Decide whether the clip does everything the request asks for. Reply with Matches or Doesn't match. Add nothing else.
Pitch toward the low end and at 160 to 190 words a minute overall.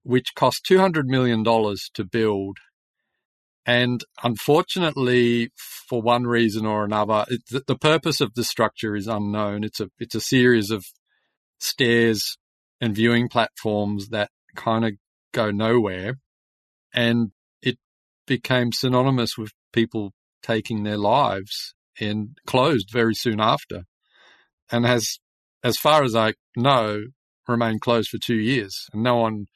Doesn't match